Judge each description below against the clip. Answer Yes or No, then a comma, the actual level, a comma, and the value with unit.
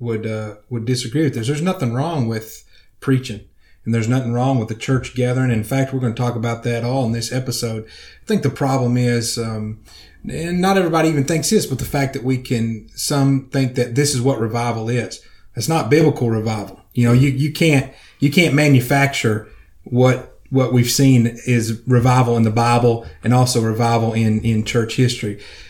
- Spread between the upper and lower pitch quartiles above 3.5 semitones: No, average, 2.9 semitones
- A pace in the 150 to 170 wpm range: No, average, 200 wpm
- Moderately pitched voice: No, low, 125 Hz